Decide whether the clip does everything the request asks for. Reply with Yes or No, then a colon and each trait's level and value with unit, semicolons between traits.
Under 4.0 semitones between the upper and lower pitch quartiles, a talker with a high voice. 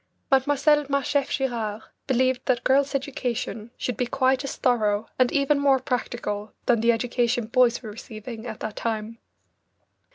Yes: average, 2.9 semitones; high, 245 Hz